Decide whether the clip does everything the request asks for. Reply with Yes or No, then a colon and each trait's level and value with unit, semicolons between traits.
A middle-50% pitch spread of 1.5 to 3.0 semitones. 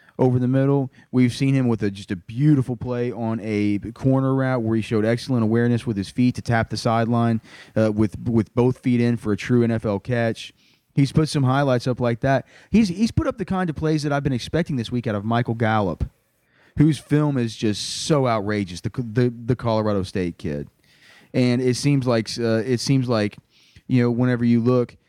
Yes: average, 2.7 semitones